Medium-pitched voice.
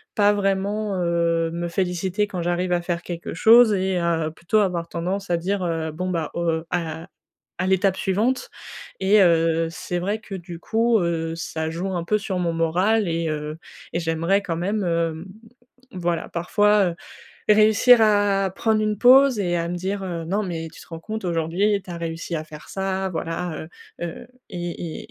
Yes: medium, 175 Hz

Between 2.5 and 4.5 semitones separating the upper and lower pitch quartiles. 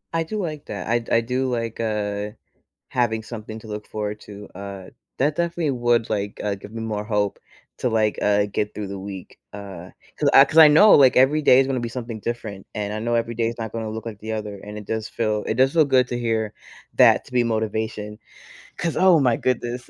Yes: average, 3.1 semitones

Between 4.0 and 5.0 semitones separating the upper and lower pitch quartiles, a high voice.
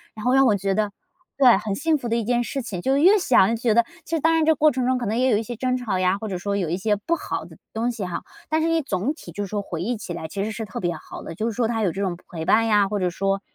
Yes: average, 4.5 semitones; high, 220 Hz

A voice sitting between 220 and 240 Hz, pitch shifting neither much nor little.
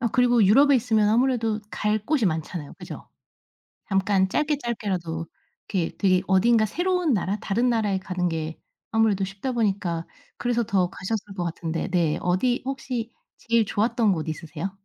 No: high, 205 Hz; average, 4.6 semitones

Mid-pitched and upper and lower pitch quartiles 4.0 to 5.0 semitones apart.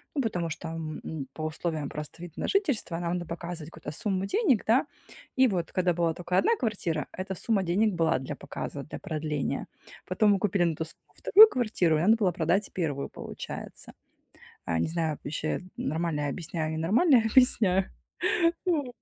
Yes: medium, 175 Hz; average, 4.7 semitones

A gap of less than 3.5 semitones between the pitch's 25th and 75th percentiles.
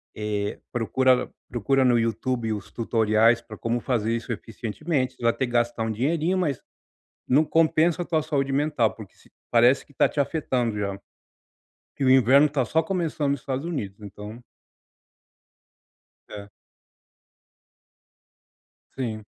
No: average, 4.2 semitones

